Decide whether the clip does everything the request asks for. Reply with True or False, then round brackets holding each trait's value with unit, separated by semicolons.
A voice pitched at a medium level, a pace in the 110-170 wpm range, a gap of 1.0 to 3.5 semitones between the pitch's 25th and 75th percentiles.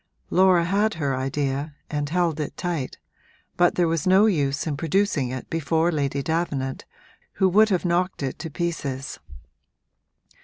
False (160 Hz; 150 wpm; 4.1 semitones)